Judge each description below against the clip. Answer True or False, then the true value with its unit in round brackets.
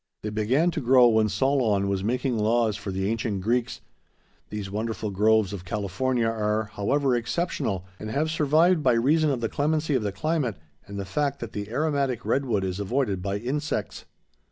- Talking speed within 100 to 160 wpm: False (180 wpm)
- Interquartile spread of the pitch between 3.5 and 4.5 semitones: False (5.0 semitones)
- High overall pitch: False (115 Hz)